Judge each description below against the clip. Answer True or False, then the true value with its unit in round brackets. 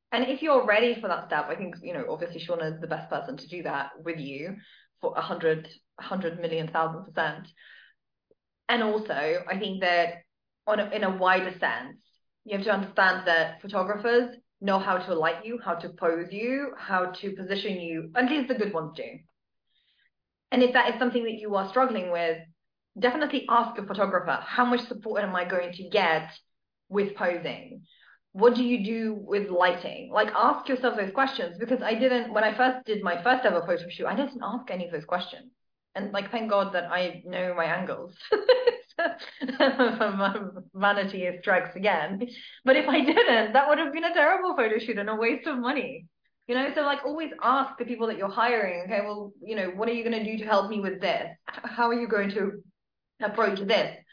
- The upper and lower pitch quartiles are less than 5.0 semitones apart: False (5.3 semitones)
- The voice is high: True (210 Hz)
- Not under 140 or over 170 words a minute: False (200 wpm)